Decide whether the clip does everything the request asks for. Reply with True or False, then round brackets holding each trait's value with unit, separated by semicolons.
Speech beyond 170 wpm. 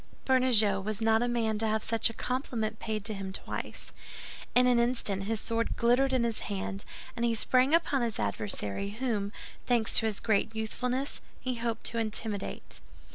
True (180 wpm)